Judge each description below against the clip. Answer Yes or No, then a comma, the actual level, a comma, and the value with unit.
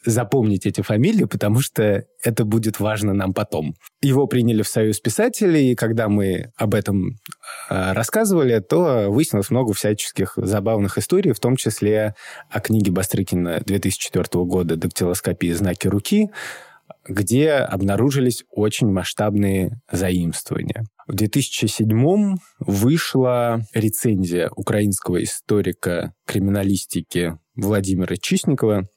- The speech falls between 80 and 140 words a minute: Yes, slow, 110 wpm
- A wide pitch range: No, average, 3.7 semitones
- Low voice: Yes, low, 105 Hz